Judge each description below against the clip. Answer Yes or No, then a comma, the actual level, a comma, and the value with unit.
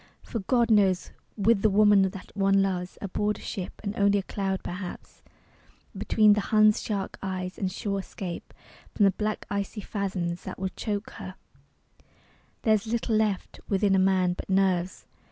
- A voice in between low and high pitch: No, high, 195 Hz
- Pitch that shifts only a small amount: Yes, narrow, 1.9 semitones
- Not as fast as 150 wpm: No, average, 165 wpm